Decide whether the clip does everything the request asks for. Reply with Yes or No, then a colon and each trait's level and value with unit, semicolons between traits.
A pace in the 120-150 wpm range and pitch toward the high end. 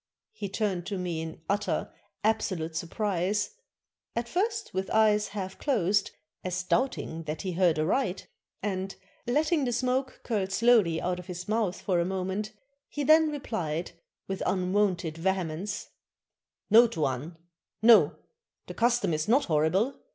Yes: average, 145 wpm; high, 195 Hz